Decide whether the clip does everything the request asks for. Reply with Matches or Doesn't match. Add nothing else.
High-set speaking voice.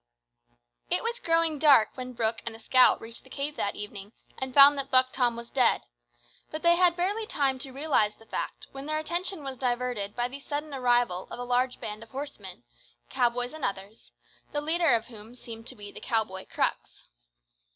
Matches